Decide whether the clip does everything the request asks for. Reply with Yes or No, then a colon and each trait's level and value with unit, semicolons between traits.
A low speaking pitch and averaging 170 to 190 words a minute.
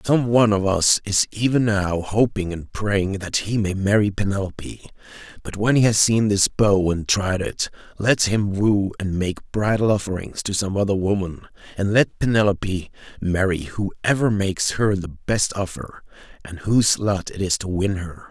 Yes: low, 100 Hz; average, 175 wpm